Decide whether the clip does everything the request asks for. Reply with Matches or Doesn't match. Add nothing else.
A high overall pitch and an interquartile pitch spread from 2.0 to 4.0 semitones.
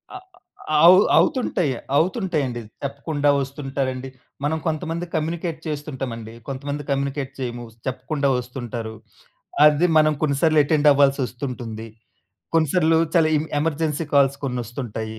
Doesn't match